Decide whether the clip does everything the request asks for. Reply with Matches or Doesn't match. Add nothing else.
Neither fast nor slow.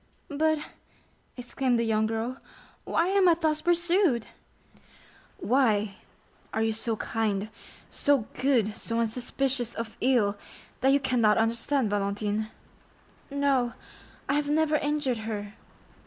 Doesn't match